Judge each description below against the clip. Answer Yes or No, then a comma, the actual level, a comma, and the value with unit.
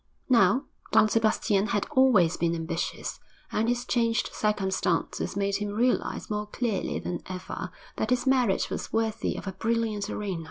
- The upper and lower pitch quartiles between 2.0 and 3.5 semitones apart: Yes, average, 3.1 semitones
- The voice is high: Yes, high, 210 Hz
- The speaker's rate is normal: Yes, average, 155 wpm